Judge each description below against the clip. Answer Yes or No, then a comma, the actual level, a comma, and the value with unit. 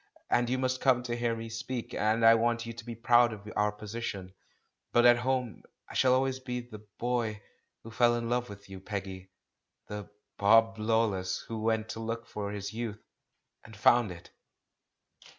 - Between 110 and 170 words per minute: No, average, 190 wpm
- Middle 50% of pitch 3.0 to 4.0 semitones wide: No, narrow, 2.4 semitones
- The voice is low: Yes, low, 115 Hz